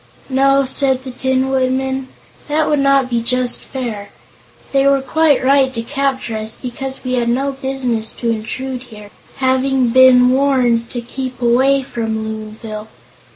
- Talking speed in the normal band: Yes, average, 155 wpm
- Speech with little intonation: Yes, narrow, 2.3 semitones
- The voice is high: Yes, very high, 260 Hz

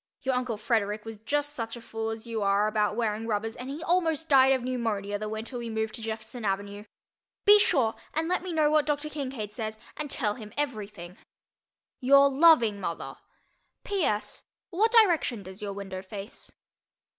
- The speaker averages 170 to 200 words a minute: Yes, average, 180 wpm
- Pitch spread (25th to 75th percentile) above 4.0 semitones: Yes, average, 5.3 semitones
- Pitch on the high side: Yes, high, 225 Hz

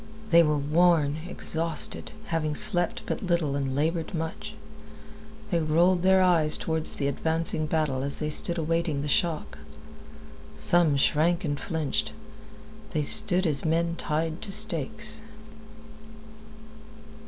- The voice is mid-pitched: Yes, medium, 165 Hz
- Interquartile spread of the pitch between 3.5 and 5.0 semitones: No, narrow, 2.5 semitones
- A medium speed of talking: No, slow, 125 wpm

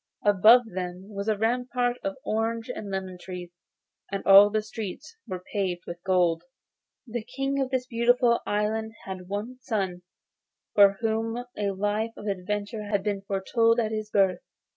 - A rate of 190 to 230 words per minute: No, average, 160 wpm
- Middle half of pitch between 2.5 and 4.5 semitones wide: Yes, average, 3.0 semitones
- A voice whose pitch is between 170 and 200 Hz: No, high, 210 Hz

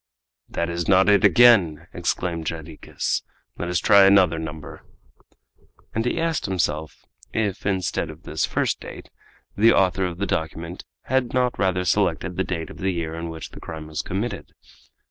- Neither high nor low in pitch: No, very low, 90 Hz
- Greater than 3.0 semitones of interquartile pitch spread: Yes, average, 3.4 semitones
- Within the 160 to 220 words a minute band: Yes, average, 165 wpm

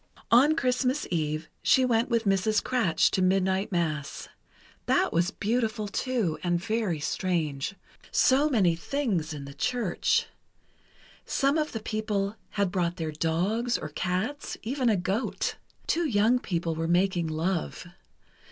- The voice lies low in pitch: No, high, 195 Hz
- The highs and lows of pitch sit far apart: Yes, wide, 5.7 semitones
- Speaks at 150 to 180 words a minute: No, average, 140 wpm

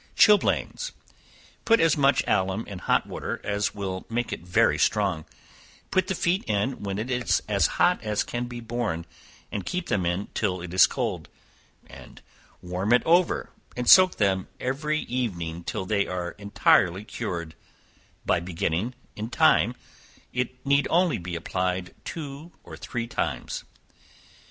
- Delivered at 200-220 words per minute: No, average, 150 wpm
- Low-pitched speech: Yes, low, 105 Hz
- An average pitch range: No, wide, 5.9 semitones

